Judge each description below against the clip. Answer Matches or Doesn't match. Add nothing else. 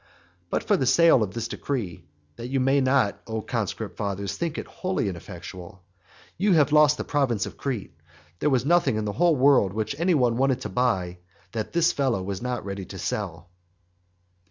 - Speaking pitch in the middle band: Doesn't match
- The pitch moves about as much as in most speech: Doesn't match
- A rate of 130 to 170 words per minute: Doesn't match